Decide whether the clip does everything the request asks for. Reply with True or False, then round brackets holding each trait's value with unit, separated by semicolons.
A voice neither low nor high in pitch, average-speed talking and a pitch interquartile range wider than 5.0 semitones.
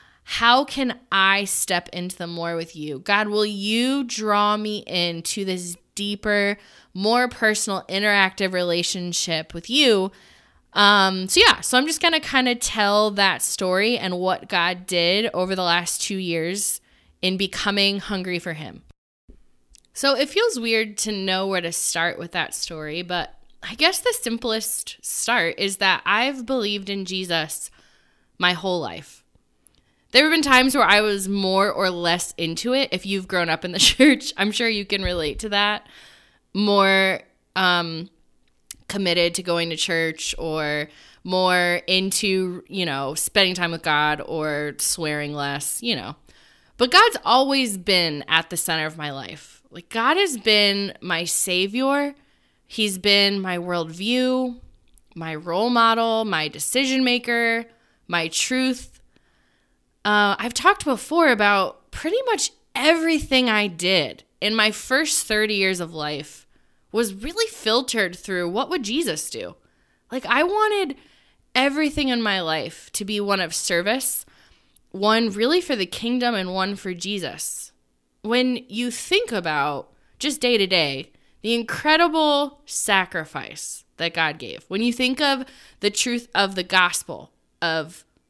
False (200 Hz; 150 wpm; 5.5 semitones)